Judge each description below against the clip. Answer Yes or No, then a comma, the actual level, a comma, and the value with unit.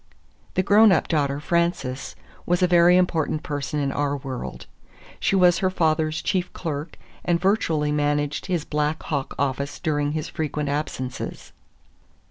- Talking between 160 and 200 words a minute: No, average, 145 wpm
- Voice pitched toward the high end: No, medium, 155 Hz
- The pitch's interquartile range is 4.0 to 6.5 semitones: No, average, 3.3 semitones